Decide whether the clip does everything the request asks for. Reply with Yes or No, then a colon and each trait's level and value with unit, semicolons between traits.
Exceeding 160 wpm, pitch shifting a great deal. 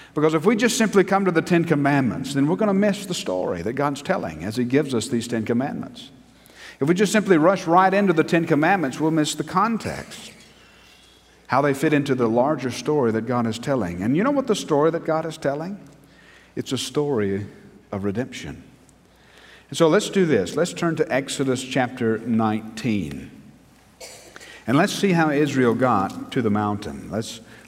Yes: average, 190 wpm; wide, 6.2 semitones